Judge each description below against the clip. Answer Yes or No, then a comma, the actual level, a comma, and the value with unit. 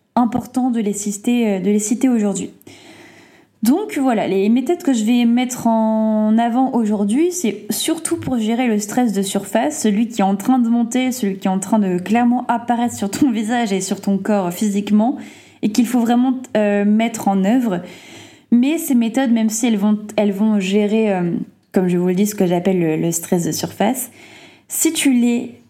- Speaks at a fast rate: No, average, 200 wpm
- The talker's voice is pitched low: No, high, 225 Hz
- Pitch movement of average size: Yes, average, 3.4 semitones